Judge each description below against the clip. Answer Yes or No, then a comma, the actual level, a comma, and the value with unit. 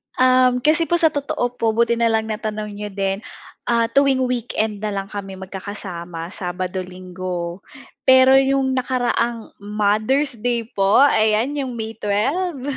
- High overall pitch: Yes, high, 220 Hz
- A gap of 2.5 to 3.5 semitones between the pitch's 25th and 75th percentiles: No, average, 4.3 semitones